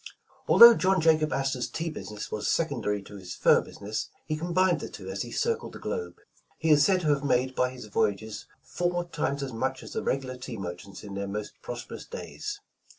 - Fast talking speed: Yes, fast, 215 wpm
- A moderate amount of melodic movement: No, wide, 7.8 semitones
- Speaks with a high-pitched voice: No, low, 135 Hz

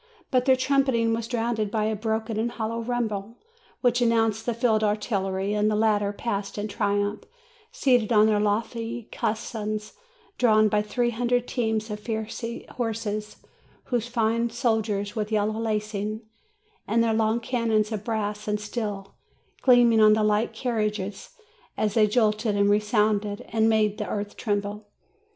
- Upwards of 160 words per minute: No, average, 150 wpm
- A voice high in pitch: Yes, high, 220 Hz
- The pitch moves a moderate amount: No, narrow, 1.7 semitones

